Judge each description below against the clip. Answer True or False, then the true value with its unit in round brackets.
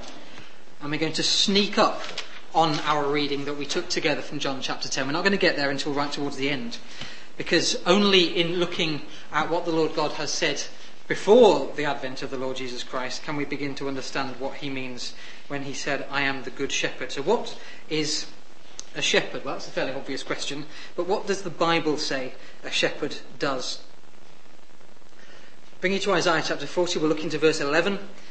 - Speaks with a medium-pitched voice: True (150 Hz)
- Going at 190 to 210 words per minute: True (200 wpm)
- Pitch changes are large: False (3.8 semitones)